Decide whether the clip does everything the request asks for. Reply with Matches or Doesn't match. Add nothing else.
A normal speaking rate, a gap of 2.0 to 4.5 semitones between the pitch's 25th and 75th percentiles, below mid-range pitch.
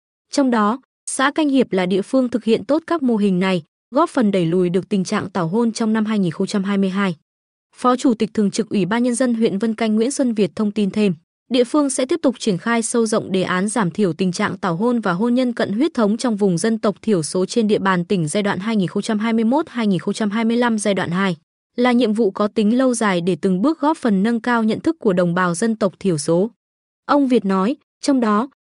Doesn't match